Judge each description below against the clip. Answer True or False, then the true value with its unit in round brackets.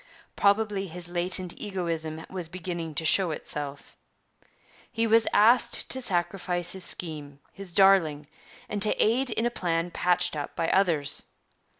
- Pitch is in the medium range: True (180 Hz)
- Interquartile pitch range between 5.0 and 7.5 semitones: False (3.4 semitones)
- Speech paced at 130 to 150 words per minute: True (140 wpm)